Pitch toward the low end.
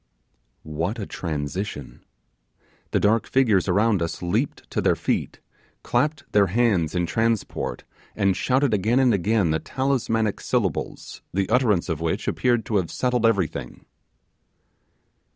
Yes: low, 105 Hz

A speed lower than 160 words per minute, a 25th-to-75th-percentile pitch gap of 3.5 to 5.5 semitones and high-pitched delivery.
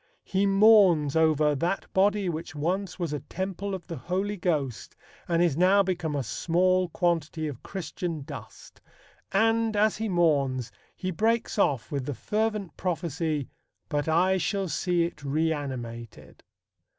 No: average, 145 wpm; average, 4.4 semitones; medium, 175 Hz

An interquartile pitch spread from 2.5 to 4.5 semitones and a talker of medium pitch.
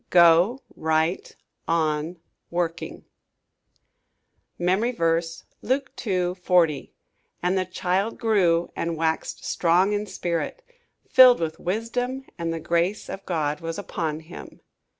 Yes: average, 3.5 semitones; medium, 175 Hz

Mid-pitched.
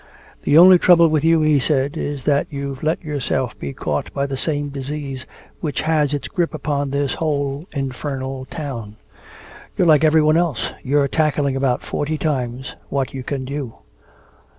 Yes: medium, 145 Hz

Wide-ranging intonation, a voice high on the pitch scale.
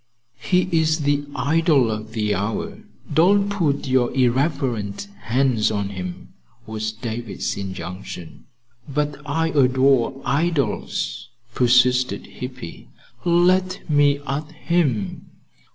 No: wide, 6.0 semitones; low, 130 Hz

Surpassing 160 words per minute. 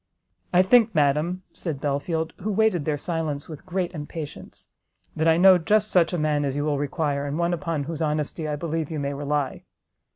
Yes: average, 195 wpm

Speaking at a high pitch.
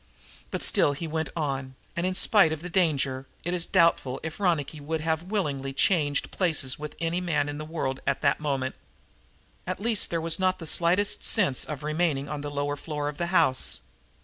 No: medium, 155 Hz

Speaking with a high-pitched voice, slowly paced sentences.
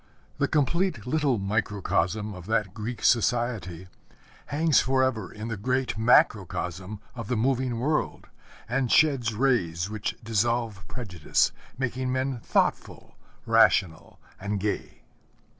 No: low, 115 Hz; slow, 115 wpm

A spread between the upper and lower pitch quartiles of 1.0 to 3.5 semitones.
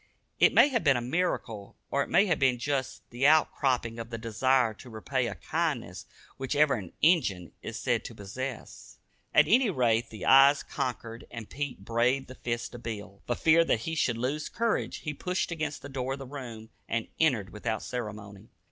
No: average, 4.2 semitones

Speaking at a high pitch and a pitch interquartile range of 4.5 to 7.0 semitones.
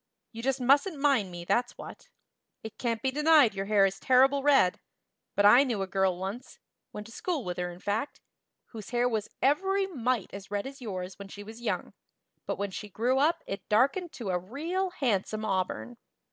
Yes: high, 230 Hz; wide, 5.5 semitones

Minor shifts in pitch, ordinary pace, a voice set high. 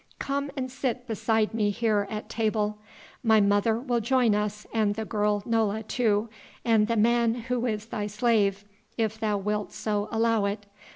Yes: narrow, 1.8 semitones; average, 170 wpm; high, 220 Hz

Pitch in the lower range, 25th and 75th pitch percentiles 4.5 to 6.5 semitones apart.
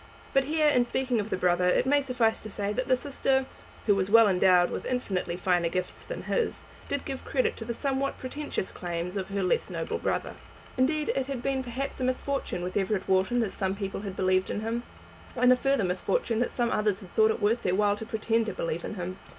No: high, 220 Hz; wide, 5.5 semitones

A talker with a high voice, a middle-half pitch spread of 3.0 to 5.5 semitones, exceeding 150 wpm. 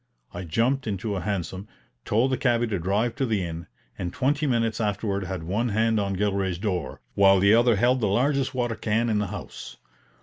No: low, 105 Hz; average, 3.6 semitones; average, 200 wpm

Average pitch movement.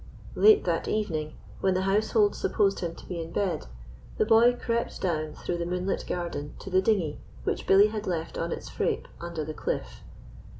Yes: average, 4.0 semitones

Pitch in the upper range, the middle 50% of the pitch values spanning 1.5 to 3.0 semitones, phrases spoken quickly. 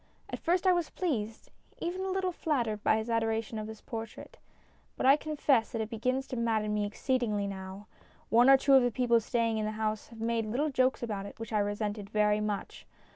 No: high, 225 Hz; average, 3.5 semitones; fast, 215 wpm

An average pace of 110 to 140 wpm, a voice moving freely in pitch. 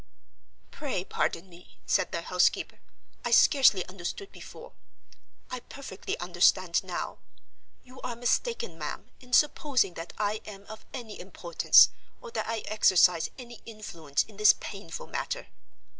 Yes: slow, 135 wpm; wide, 5.8 semitones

